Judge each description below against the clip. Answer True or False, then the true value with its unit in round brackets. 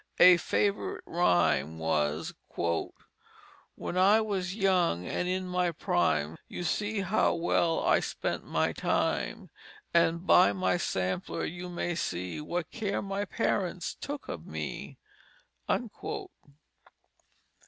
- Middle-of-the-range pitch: True (175 Hz)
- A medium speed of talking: False (115 wpm)